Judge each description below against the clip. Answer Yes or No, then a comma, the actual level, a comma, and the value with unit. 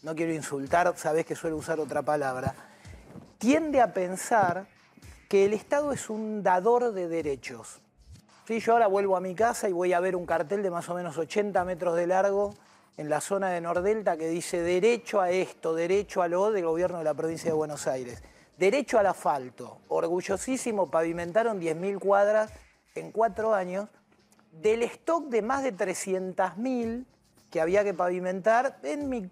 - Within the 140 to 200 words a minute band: Yes, average, 170 wpm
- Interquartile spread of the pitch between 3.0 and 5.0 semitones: Yes, average, 4.6 semitones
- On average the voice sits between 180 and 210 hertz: Yes, medium, 185 Hz